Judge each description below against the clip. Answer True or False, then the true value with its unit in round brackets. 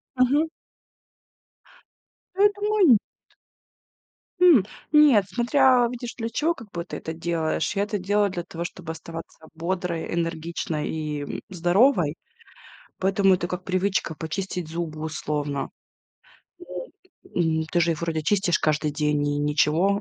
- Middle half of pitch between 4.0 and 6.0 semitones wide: True (4.8 semitones)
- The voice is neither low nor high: True (175 Hz)